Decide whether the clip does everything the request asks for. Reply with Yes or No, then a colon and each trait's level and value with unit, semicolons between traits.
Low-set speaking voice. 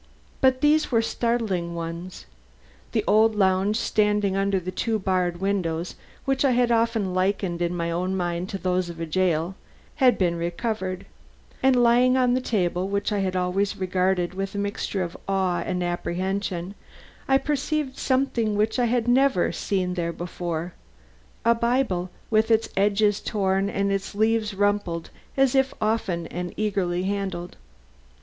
No: high, 195 Hz